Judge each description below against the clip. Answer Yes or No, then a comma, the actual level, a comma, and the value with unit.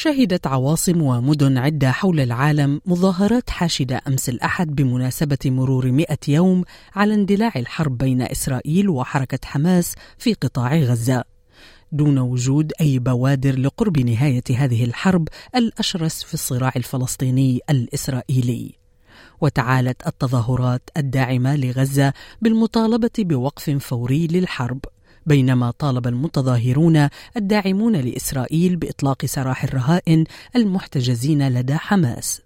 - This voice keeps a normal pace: Yes, average, 105 wpm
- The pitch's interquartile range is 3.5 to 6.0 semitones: Yes, average, 4.5 semitones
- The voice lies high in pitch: No, medium, 140 Hz